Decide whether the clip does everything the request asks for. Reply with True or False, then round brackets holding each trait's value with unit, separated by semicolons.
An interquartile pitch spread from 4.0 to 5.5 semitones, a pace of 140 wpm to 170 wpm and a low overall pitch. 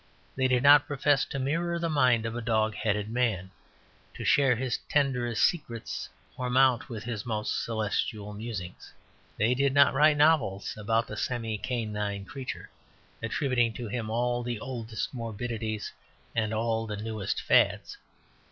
False (3.2 semitones; 150 wpm; 115 Hz)